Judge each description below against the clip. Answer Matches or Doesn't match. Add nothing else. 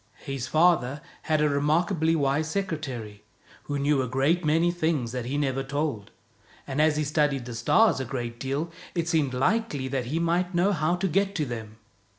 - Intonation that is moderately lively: Matches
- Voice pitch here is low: Doesn't match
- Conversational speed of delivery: Matches